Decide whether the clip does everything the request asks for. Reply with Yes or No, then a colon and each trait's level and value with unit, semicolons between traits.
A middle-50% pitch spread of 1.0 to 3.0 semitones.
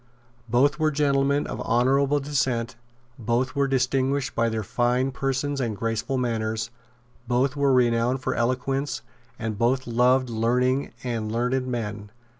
Yes: narrow, 2.6 semitones